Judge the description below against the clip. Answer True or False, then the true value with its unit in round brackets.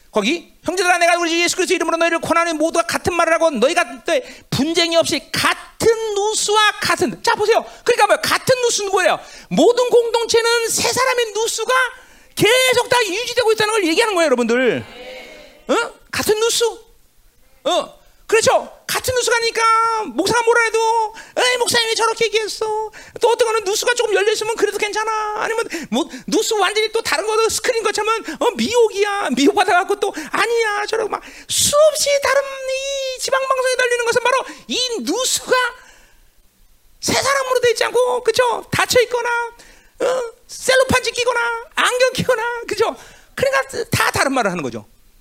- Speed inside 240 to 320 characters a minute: False (355 characters per minute)